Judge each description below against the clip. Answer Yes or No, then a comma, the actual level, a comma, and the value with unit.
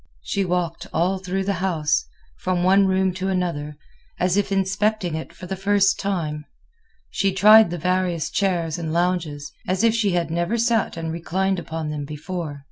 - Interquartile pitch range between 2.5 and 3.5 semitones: Yes, average, 2.8 semitones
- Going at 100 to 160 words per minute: No, average, 175 wpm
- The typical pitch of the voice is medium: Yes, medium, 180 Hz